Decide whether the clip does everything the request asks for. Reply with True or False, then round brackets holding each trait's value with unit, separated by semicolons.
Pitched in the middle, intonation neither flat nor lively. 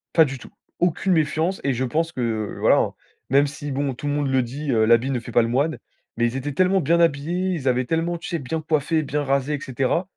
True (145 Hz; 4.0 semitones)